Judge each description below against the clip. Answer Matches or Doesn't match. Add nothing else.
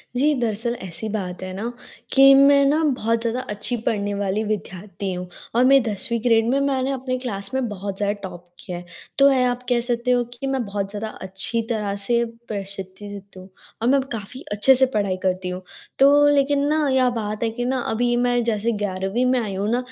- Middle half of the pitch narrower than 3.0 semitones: Doesn't match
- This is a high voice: Matches